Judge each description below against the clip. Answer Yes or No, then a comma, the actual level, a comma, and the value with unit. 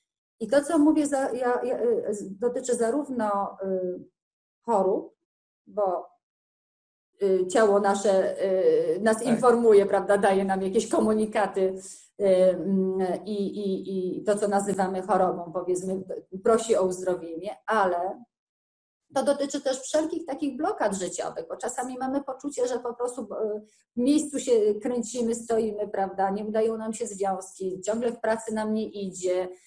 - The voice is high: Yes, high, 215 Hz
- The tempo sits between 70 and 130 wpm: Yes, average, 125 wpm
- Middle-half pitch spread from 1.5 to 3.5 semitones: No, average, 4.9 semitones